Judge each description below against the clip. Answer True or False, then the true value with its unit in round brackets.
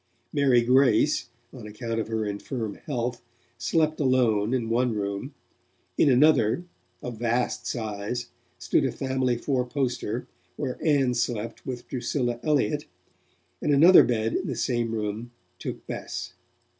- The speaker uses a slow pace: True (130 wpm)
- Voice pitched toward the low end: True (120 Hz)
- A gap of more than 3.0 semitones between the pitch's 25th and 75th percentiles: False (2.7 semitones)